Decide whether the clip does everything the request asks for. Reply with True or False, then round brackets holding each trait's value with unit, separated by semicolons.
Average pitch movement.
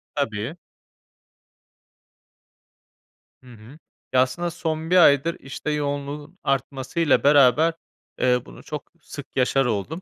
True (3.5 semitones)